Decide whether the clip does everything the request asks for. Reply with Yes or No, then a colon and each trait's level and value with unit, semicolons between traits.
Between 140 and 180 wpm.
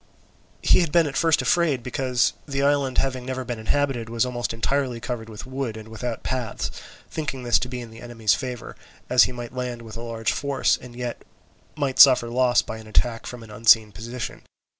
No: fast, 205 wpm